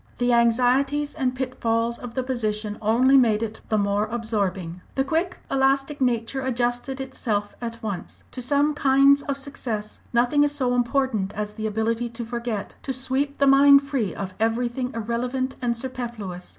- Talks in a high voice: Yes, high, 245 Hz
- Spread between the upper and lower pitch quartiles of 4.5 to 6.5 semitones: No, average, 3.3 semitones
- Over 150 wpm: Yes, average, 165 wpm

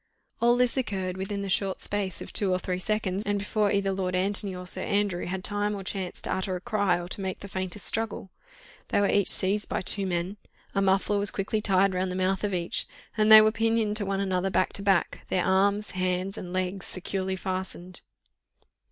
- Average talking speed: No, fast, 215 wpm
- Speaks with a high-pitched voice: Yes, high, 195 Hz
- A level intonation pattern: Yes, narrow, 1.8 semitones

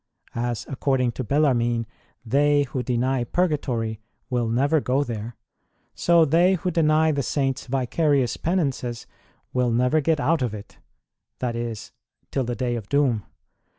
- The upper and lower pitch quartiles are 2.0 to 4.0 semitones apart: Yes, average, 3.6 semitones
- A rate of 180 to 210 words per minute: No, average, 140 wpm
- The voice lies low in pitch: Yes, low, 130 Hz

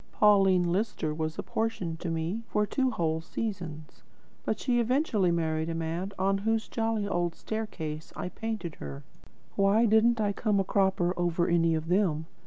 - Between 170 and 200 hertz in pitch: Yes, medium, 185 Hz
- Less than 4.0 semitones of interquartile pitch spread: No, average, 4.8 semitones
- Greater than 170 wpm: No, average, 165 wpm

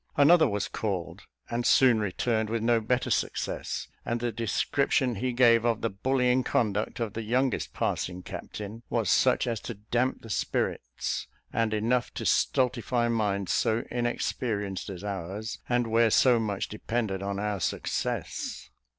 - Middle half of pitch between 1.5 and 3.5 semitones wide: Yes, average, 2.9 semitones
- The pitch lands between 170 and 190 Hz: No, low, 115 Hz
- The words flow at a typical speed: Yes, average, 150 wpm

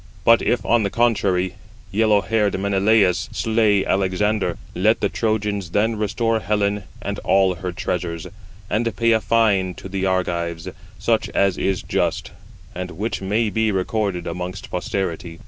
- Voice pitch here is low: Yes, low, 100 Hz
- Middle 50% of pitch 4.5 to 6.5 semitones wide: No, average, 3.0 semitones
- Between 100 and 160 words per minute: Yes, average, 145 wpm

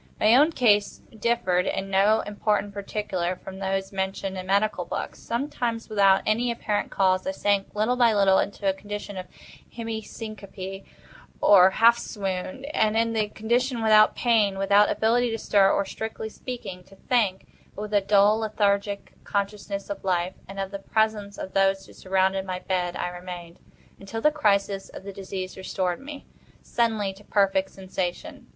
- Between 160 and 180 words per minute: Yes, average, 170 wpm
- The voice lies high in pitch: Yes, high, 200 Hz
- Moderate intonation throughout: No, narrow, 2.3 semitones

